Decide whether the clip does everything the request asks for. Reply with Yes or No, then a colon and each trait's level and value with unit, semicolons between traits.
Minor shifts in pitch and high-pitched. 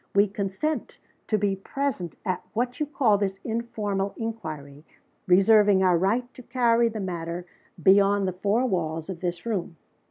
No: average, 3.9 semitones; high, 200 Hz